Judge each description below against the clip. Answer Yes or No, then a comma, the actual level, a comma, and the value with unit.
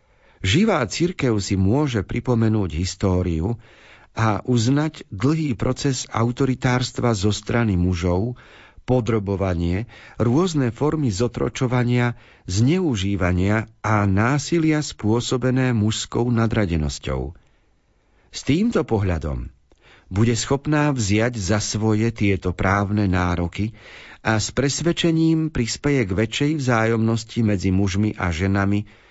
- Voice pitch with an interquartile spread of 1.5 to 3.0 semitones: No, average, 4.1 semitones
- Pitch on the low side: Yes, low, 110 Hz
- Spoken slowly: Yes, slow, 95 wpm